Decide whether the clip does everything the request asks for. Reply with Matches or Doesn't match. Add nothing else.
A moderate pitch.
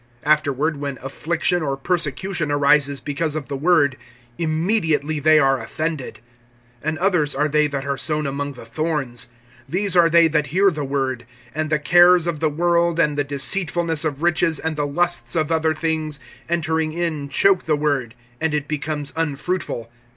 Matches